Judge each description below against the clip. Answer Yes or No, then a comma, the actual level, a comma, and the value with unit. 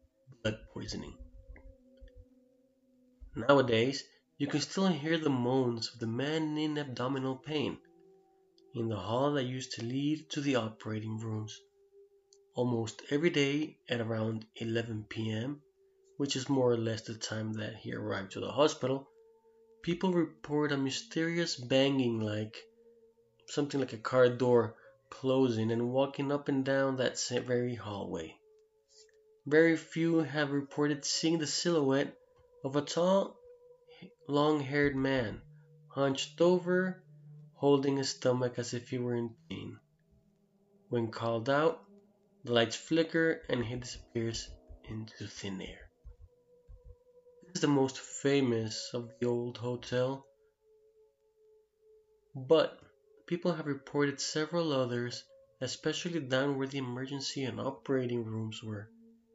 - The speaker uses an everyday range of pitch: No, wide, 6.2 semitones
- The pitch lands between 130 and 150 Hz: Yes, medium, 140 Hz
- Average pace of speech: No, slow, 125 wpm